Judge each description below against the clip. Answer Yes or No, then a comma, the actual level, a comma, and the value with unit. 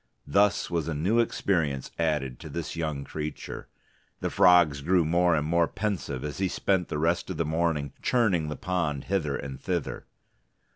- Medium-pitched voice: No, very low, 80 Hz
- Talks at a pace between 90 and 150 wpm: No, average, 175 wpm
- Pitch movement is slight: No, average, 3.3 semitones